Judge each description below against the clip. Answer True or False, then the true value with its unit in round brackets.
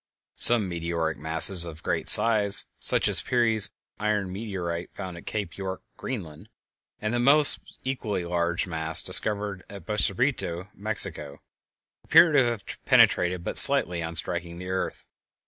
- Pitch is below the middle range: True (95 Hz)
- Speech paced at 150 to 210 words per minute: False (140 wpm)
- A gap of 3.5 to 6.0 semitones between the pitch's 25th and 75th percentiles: True (4.1 semitones)